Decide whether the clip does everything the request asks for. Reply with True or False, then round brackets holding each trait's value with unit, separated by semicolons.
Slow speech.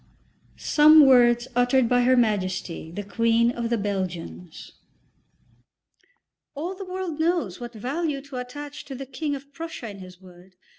False (155 wpm)